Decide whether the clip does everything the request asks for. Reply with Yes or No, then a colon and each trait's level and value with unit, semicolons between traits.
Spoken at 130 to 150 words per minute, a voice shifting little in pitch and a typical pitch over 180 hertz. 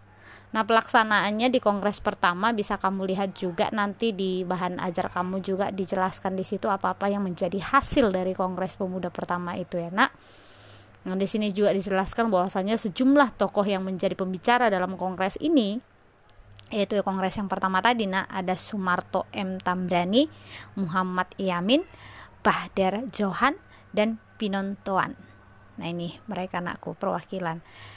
Yes: fast, 140 wpm; narrow, 2.3 semitones; high, 190 Hz